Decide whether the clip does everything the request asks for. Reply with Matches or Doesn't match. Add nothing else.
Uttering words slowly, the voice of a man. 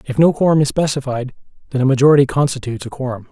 Doesn't match